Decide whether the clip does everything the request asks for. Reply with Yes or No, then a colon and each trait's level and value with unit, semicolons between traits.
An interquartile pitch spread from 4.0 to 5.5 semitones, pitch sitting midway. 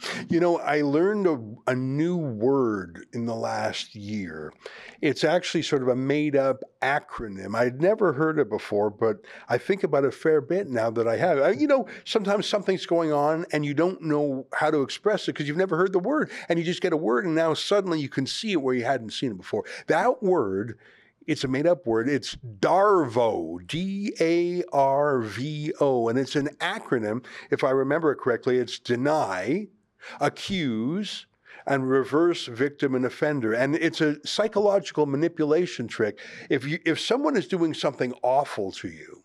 Yes: average, 5.2 semitones; medium, 150 Hz